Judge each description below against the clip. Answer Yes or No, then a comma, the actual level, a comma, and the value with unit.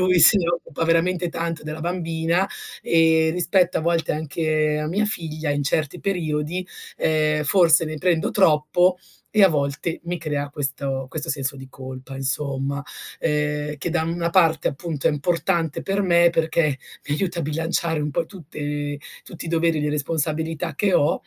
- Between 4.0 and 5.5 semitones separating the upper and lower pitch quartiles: No, narrow, 2.4 semitones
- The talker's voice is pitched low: No, medium, 160 Hz